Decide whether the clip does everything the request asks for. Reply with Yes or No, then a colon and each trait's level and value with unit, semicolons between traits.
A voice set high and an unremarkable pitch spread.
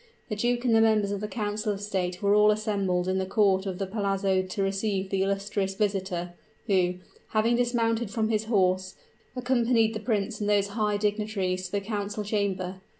No: high, 205 Hz; narrow, 2.1 semitones